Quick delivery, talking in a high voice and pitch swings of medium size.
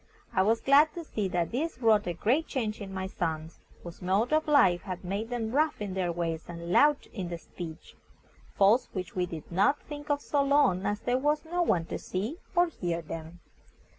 No: fast, 210 wpm; high, 205 Hz; wide, 8.2 semitones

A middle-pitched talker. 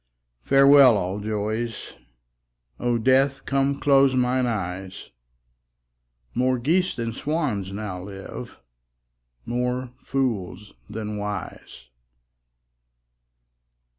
No: low, 120 Hz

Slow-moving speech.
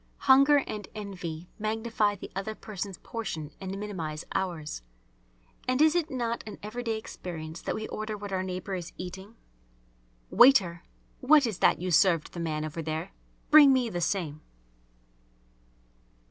No: average, 145 wpm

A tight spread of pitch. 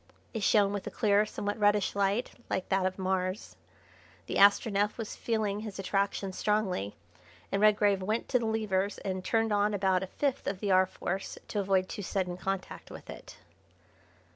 Yes: narrow, 1.9 semitones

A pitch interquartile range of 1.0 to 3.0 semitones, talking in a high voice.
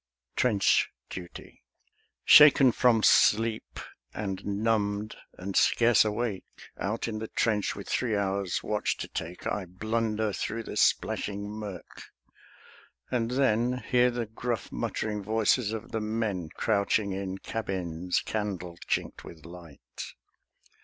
No: average, 2.7 semitones; low, 105 Hz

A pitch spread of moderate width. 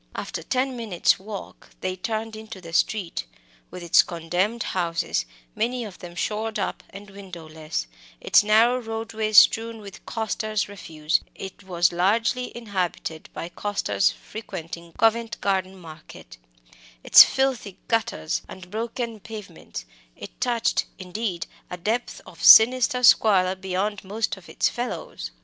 Yes: average, 4.0 semitones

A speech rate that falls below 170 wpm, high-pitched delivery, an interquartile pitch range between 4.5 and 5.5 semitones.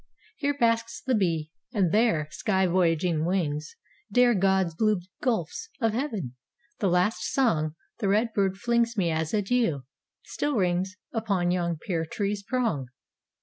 Yes: average, 145 wpm; high, 195 Hz; average, 5.1 semitones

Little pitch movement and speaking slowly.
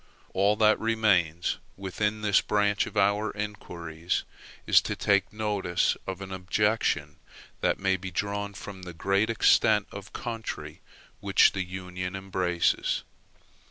Yes: narrow, 2.3 semitones; slow, 130 wpm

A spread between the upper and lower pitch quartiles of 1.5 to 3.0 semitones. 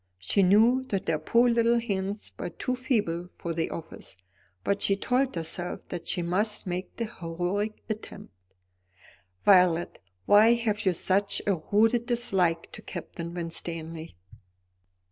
No: average, 4.8 semitones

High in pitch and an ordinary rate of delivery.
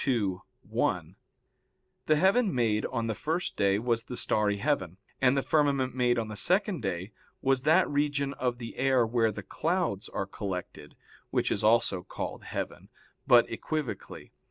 No: low, 120 Hz; average, 160 wpm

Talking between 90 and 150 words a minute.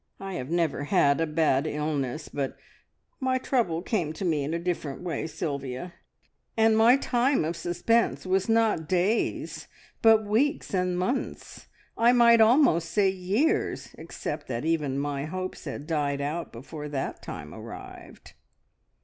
Yes: average, 145 wpm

